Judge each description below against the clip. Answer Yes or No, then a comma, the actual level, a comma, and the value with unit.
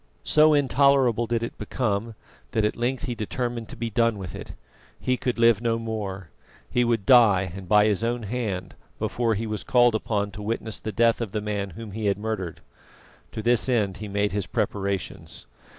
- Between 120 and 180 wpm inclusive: No, average, 195 wpm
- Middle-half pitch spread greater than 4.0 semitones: No, average, 2.7 semitones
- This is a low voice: Yes, low, 110 Hz